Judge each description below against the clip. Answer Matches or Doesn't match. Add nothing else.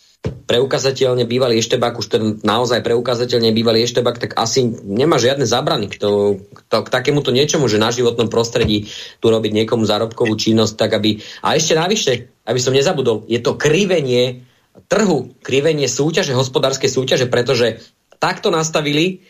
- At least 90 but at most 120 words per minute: Doesn't match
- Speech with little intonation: Doesn't match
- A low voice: Matches